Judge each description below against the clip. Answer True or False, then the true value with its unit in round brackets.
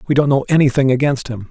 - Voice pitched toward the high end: False (135 Hz)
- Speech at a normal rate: False (240 wpm)